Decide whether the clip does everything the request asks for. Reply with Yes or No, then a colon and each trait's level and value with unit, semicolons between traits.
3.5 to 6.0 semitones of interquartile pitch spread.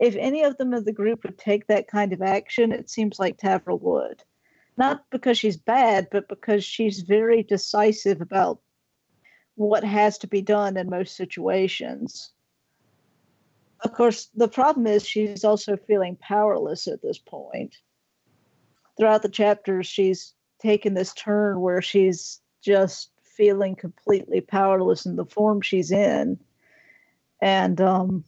No: average, 2.8 semitones